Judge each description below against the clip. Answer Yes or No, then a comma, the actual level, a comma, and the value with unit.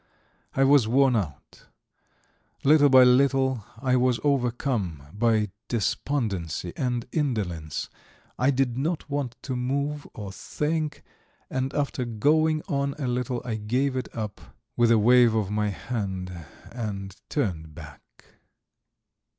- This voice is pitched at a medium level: No, low, 125 Hz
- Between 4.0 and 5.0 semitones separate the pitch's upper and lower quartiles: Yes, average, 4.7 semitones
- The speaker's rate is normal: No, slow, 125 wpm